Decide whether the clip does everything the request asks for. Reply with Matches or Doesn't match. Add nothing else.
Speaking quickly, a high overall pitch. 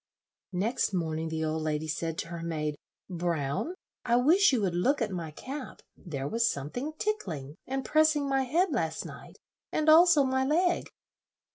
Doesn't match